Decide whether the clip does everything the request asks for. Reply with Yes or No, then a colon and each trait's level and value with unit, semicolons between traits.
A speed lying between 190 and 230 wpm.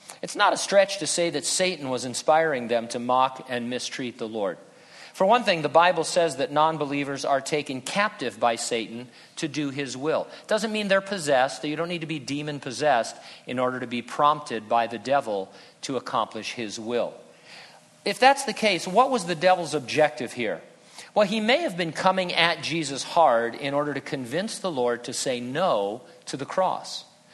Yes: average, 200 wpm